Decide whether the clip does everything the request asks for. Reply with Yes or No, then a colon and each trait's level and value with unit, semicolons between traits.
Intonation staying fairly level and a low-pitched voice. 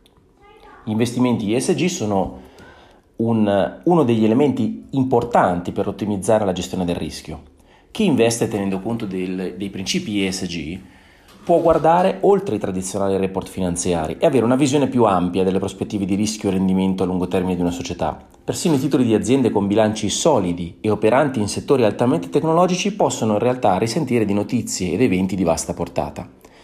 No: average, 4.1 semitones; low, 100 Hz